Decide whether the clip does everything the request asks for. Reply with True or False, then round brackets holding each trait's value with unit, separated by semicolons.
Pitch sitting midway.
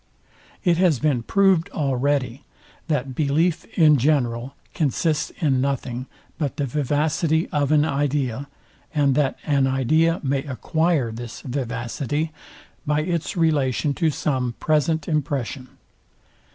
True (145 Hz)